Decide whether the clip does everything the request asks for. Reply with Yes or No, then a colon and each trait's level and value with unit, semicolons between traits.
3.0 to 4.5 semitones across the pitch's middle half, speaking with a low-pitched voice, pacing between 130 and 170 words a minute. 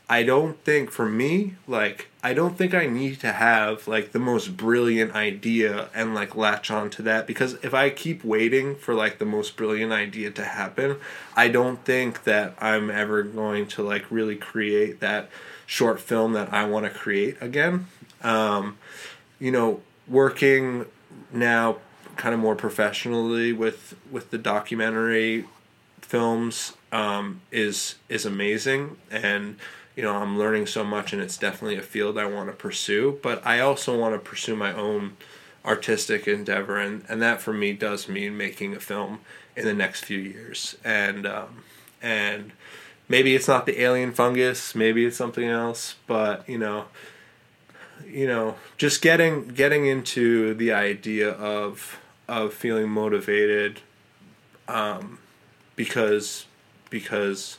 Yes: average, 3.4 semitones; low, 110 Hz; average, 155 wpm